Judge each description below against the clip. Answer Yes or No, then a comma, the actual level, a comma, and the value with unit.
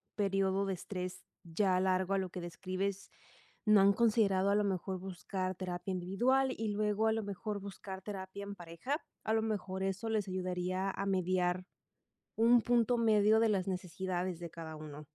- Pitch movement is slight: Yes, narrow, 2.2 semitones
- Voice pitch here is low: No, high, 195 Hz